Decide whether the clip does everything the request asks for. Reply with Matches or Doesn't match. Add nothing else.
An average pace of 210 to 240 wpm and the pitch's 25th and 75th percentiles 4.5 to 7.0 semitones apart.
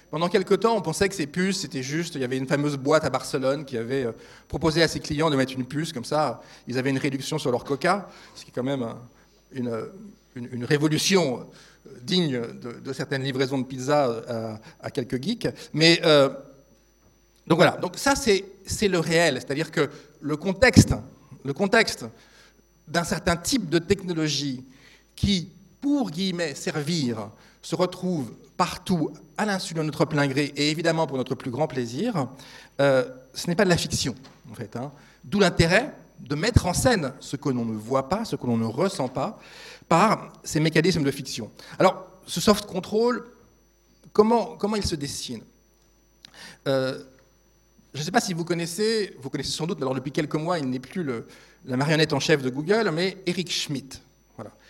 Doesn't match